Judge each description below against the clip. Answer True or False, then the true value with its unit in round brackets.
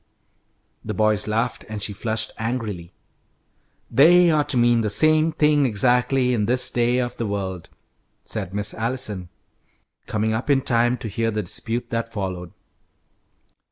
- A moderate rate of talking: True (150 wpm)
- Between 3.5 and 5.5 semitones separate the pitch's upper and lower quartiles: False (3.1 semitones)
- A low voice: True (115 Hz)